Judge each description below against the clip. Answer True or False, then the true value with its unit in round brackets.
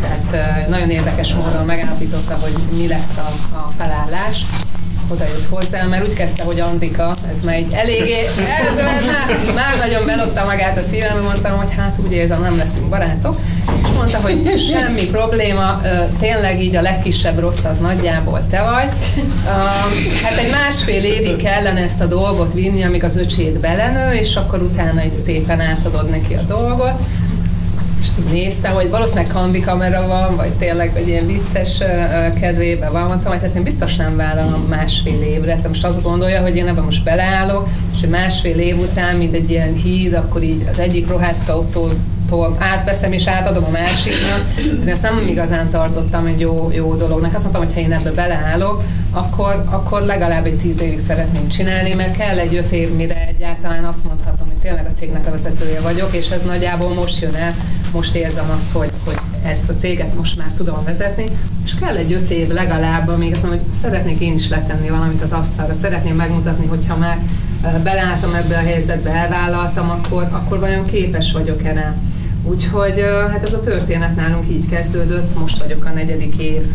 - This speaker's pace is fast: True (175 wpm)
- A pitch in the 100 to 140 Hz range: False (90 Hz)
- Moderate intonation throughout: False (1.6 semitones)